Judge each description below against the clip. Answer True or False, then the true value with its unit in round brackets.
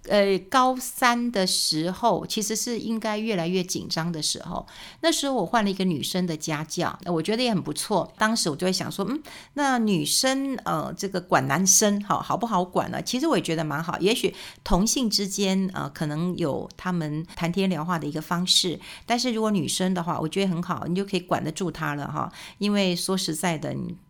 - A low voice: False (185 Hz)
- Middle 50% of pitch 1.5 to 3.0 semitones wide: False (4.4 semitones)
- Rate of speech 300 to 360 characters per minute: True (305 characters per minute)